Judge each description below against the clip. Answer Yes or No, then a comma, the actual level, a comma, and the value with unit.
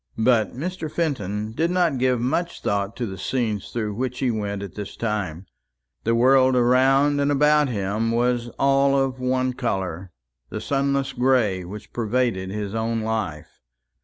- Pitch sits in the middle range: No, low, 120 Hz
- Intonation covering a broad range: No, average, 4.4 semitones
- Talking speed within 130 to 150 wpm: No, average, 160 wpm